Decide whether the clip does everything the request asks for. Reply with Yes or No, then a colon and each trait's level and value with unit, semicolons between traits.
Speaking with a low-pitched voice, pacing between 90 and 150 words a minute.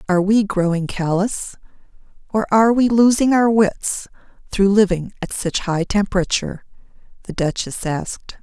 No: high, 200 Hz; slow, 135 wpm